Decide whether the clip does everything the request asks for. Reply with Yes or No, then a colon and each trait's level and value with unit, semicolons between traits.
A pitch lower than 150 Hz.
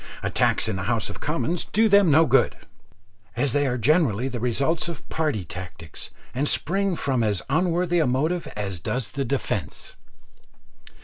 Yes: medium, 140 Hz